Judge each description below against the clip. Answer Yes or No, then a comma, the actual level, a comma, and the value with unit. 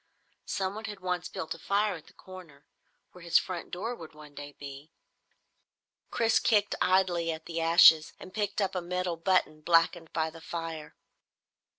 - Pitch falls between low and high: Yes, medium, 170 Hz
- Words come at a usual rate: Yes, average, 170 wpm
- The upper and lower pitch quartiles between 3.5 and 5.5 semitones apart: No, average, 2.8 semitones